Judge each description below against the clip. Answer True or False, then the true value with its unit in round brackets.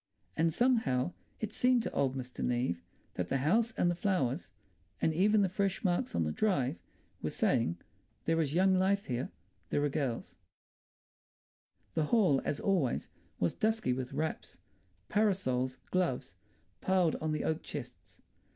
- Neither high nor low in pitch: True (160 Hz)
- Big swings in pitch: True (6.9 semitones)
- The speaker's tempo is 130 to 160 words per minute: True (150 wpm)